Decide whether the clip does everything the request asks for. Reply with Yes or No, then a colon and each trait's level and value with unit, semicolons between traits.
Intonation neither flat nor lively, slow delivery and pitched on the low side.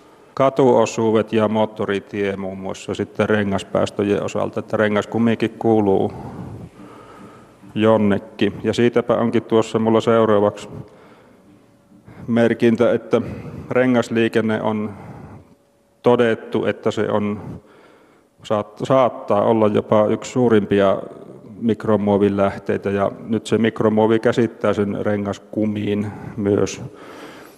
No: narrow, 1.8 semitones; slow, 90 wpm; low, 110 Hz